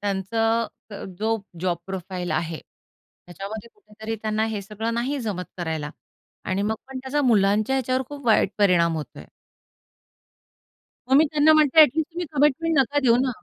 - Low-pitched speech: No, high, 220 Hz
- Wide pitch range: Yes, wide, 5.7 semitones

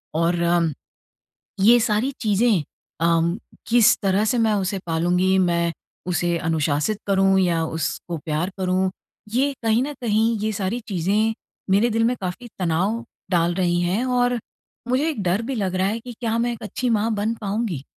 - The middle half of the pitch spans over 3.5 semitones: Yes, average, 4.7 semitones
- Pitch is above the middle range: Yes, high, 195 Hz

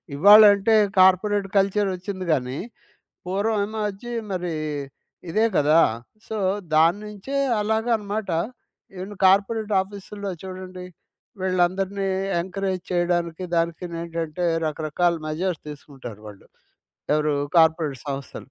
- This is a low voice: No, medium, 185 Hz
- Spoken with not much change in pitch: No, average, 3.5 semitones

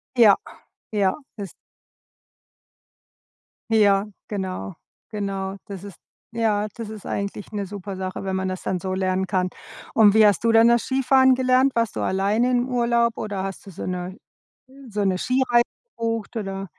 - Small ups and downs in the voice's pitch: No, average, 3.3 semitones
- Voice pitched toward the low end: No, high, 205 Hz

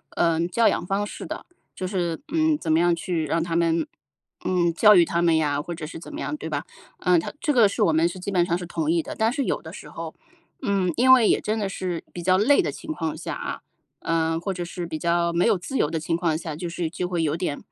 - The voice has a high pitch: No, medium, 175 Hz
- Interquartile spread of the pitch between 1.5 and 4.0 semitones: Yes, average, 3.0 semitones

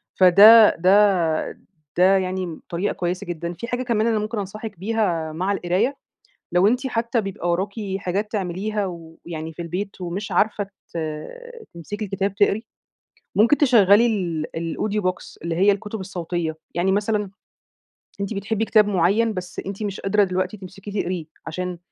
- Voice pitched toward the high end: Yes, high, 195 Hz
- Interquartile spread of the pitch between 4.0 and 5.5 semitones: No, average, 3.1 semitones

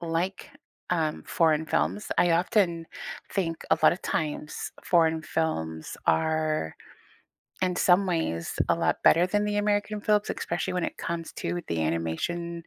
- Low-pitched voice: No, medium, 165 Hz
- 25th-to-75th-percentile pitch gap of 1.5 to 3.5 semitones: Yes, average, 2.7 semitones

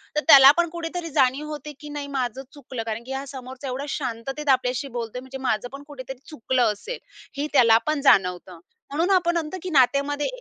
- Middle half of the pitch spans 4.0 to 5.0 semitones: No, average, 3.2 semitones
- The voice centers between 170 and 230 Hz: No, very high, 270 Hz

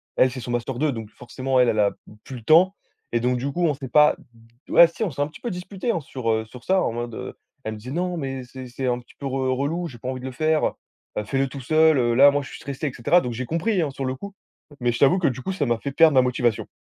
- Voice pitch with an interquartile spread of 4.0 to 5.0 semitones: Yes, average, 4.3 semitones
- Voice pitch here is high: No, low, 135 Hz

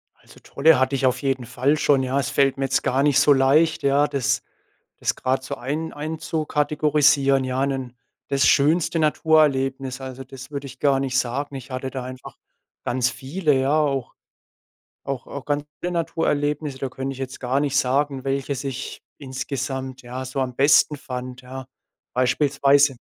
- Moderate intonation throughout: No, narrow, 1.8 semitones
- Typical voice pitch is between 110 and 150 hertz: Yes, low, 135 Hz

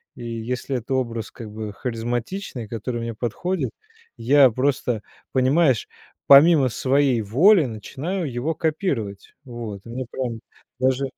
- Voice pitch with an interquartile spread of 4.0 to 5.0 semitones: No, average, 3.5 semitones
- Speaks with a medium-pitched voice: No, low, 125 Hz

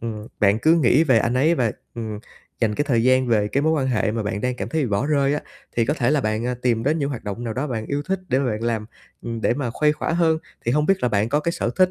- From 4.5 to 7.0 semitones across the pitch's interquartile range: Yes, average, 4.8 semitones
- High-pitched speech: No, low, 125 Hz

